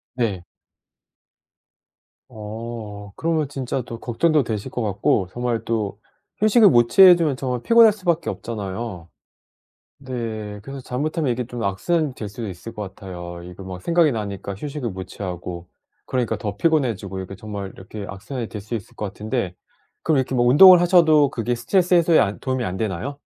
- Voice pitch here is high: No, low, 115 Hz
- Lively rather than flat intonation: Yes, wide, 5.9 semitones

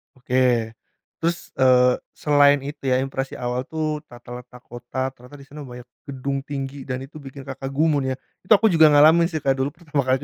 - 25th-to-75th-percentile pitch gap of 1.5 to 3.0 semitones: Yes, narrow, 2.5 semitones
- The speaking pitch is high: No, low, 135 Hz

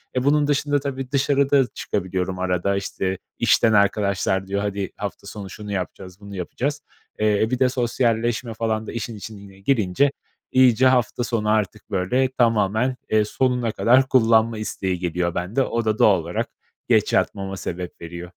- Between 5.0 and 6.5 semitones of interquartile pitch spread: No, average, 4.6 semitones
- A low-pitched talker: Yes, low, 110 Hz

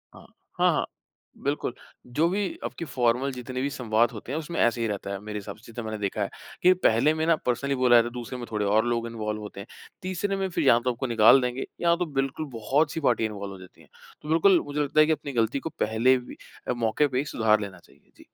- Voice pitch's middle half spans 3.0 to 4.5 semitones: No, average, 5.0 semitones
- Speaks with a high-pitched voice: No, low, 125 Hz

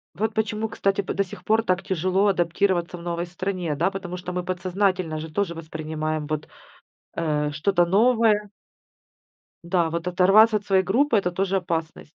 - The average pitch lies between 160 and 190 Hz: Yes, medium, 185 Hz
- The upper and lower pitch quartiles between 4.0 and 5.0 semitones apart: No, average, 2.9 semitones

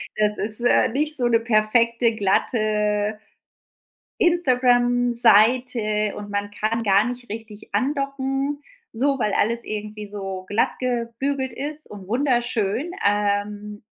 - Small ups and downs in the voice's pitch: No, average, 3.2 semitones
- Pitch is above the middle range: Yes, high, 230 Hz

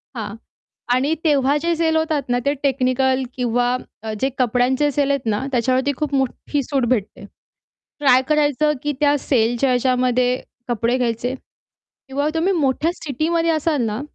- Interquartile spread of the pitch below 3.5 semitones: Yes, average, 3.0 semitones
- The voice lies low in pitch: No, very high, 265 Hz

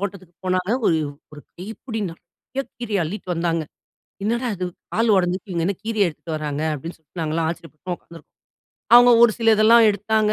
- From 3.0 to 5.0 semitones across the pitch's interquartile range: Yes, average, 4.7 semitones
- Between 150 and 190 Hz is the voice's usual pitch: Yes, medium, 185 Hz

